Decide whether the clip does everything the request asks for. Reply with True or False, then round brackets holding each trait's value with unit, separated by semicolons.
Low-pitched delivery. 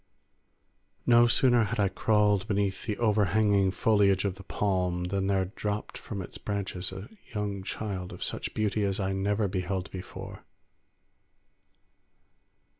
True (100 Hz)